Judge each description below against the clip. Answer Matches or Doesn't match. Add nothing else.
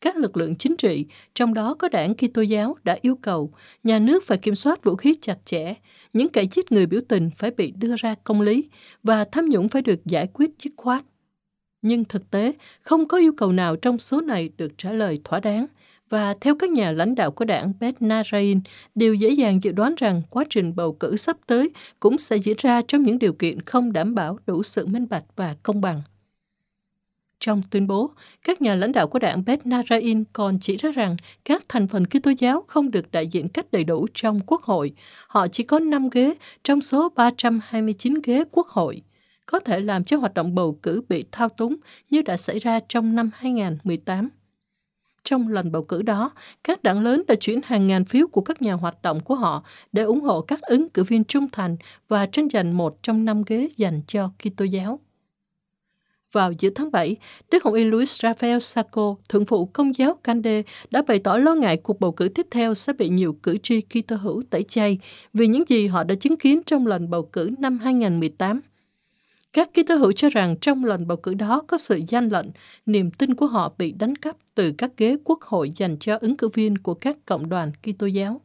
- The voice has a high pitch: Matches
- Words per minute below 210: Doesn't match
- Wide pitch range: Doesn't match